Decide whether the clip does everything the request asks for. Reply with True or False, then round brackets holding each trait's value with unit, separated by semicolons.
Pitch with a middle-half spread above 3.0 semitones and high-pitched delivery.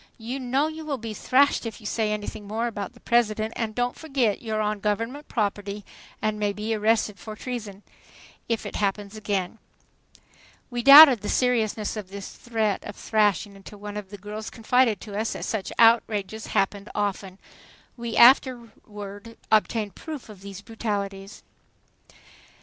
False (2.4 semitones; 215 Hz)